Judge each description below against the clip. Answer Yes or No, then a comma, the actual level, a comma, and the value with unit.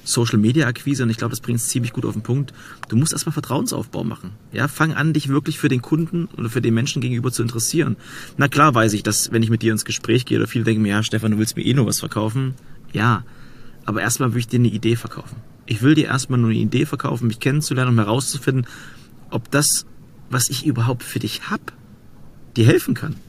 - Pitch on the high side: No, low, 125 Hz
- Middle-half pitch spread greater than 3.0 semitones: Yes, average, 3.6 semitones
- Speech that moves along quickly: Yes, fast, 235 wpm